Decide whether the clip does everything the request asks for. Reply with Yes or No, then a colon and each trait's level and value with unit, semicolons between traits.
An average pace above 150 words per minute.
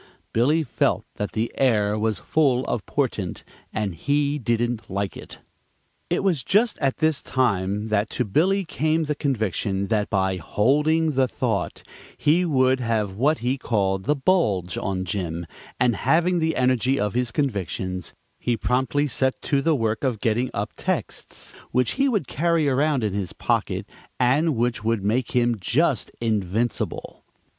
Yes: average, 160 wpm